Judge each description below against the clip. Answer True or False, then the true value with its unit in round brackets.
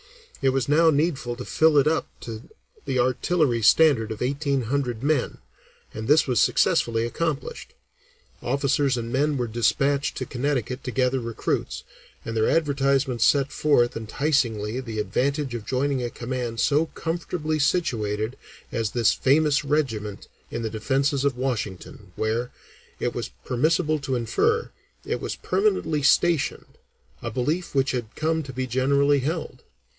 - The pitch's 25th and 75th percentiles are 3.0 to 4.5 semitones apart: True (3.8 semitones)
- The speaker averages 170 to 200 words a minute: False (150 wpm)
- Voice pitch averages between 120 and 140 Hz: True (135 Hz)